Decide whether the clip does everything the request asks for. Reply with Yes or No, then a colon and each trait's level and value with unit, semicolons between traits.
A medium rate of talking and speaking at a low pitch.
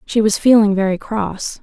No: average, 185 wpm; high, 205 Hz